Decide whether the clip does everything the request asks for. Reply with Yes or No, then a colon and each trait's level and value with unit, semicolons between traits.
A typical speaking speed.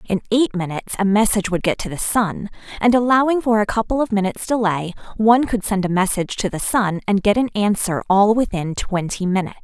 No: fast, 210 wpm